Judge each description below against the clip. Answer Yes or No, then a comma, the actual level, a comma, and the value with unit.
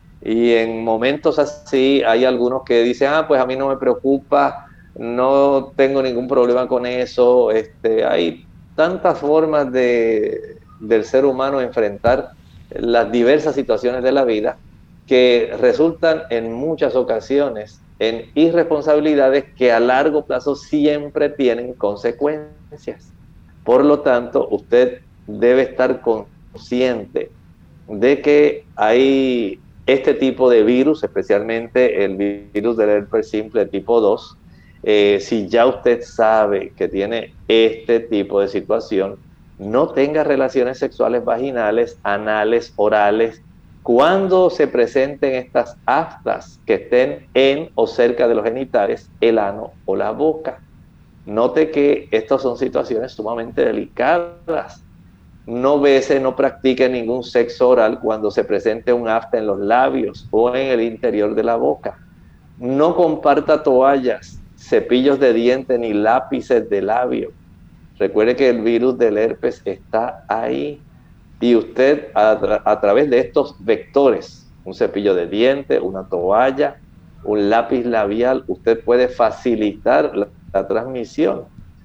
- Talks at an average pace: No, slow, 130 wpm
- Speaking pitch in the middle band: No, low, 125 Hz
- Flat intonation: No, average, 3.9 semitones